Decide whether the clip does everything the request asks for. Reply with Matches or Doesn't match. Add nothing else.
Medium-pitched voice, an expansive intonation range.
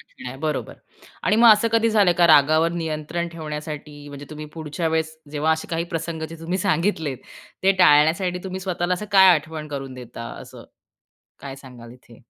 Doesn't match